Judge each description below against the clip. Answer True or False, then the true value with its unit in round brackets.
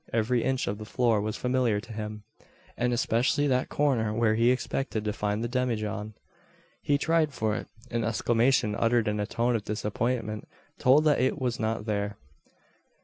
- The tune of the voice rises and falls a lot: False (2.9 semitones)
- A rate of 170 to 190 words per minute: True (175 wpm)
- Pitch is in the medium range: False (115 Hz)